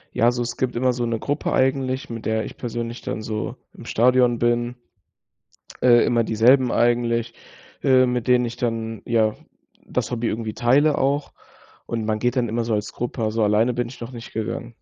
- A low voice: Yes, low, 120 Hz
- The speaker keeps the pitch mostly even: Yes, narrow, 1.6 semitones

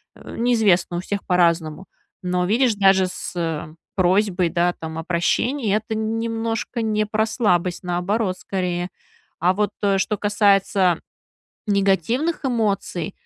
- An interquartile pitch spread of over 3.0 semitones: Yes, average, 3.6 semitones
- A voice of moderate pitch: No, high, 195 Hz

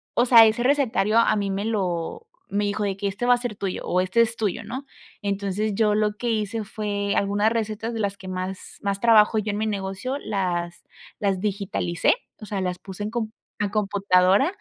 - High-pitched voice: Yes, high, 205 Hz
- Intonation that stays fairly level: Yes, narrow, 2.2 semitones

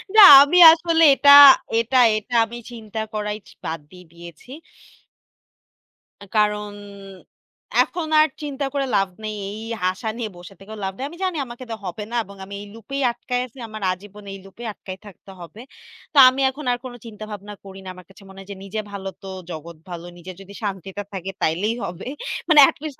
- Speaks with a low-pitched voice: No, high, 210 Hz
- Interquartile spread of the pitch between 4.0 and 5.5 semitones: Yes, average, 4.4 semitones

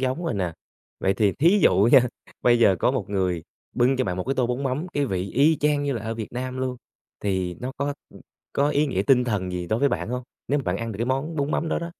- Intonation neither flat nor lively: No, wide, 5.8 semitones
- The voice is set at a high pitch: No, low, 125 Hz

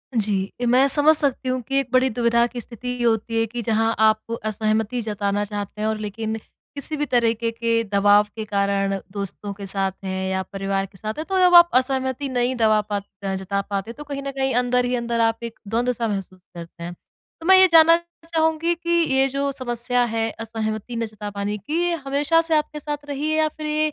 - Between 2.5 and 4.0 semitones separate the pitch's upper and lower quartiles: No, average, 4.8 semitones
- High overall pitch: Yes, high, 230 Hz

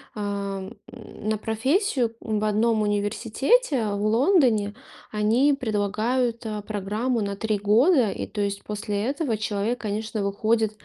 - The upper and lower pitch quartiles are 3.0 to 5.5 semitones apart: No, narrow, 2.5 semitones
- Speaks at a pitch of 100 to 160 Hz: No, high, 215 Hz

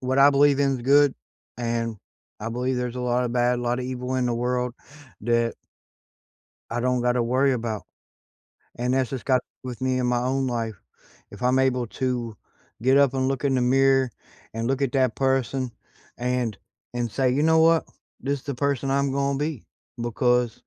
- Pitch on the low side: Yes, low, 125 Hz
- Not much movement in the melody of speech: Yes, narrow, 1.8 semitones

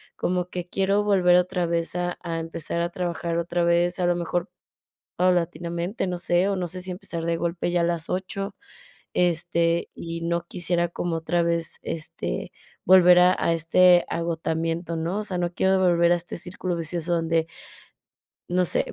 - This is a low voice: No, medium, 175 Hz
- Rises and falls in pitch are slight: Yes, narrow, 1.2 semitones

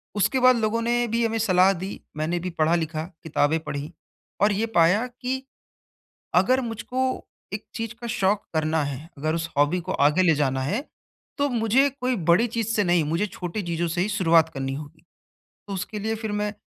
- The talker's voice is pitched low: No, high, 190 Hz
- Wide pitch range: Yes, wide, 5.8 semitones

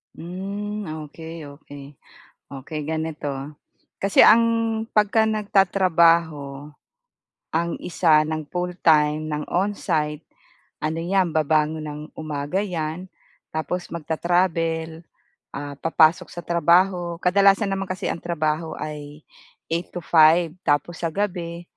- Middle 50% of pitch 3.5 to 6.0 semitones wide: No, average, 2.9 semitones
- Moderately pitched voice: Yes, medium, 165 Hz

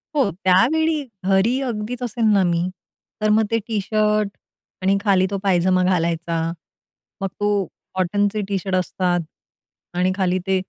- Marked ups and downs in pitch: No, narrow, 2.6 semitones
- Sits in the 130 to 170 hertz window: No, high, 195 Hz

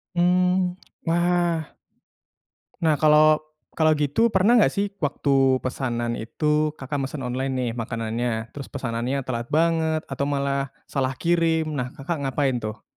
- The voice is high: No, medium, 145 Hz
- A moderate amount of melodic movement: Yes, average, 4.2 semitones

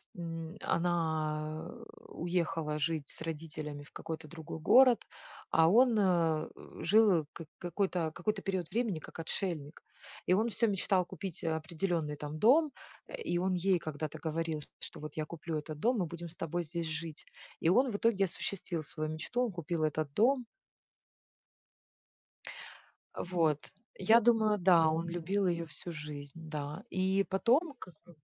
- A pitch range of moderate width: Yes, average, 3.8 semitones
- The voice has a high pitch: No, medium, 170 Hz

